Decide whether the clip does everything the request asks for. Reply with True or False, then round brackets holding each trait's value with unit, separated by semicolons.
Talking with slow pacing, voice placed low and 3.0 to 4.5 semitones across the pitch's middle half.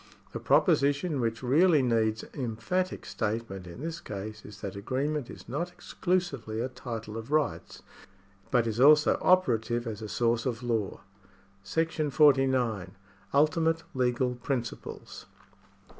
False (130 wpm; 125 Hz; 5.0 semitones)